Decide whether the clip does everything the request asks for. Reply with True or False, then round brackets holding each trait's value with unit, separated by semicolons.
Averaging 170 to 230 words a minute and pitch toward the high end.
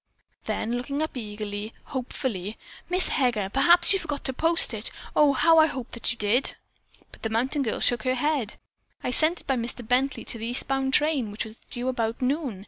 True (200 wpm; 255 Hz)